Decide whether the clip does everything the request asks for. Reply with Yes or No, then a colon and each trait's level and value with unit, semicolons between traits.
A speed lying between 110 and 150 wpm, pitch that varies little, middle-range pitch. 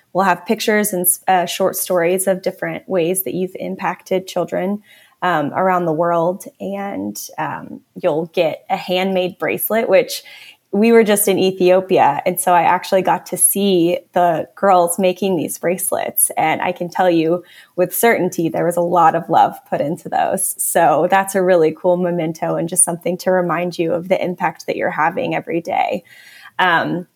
No: average, 175 wpm; narrow, 1.5 semitones; medium, 180 Hz